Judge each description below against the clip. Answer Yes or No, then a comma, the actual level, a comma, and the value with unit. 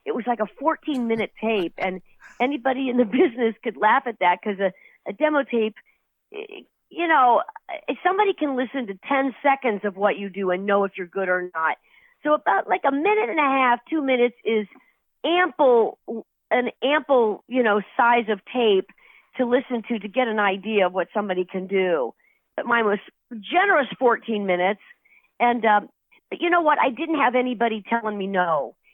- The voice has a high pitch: Yes, high, 240 Hz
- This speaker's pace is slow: No, average, 190 wpm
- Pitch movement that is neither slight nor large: No, wide, 6.1 semitones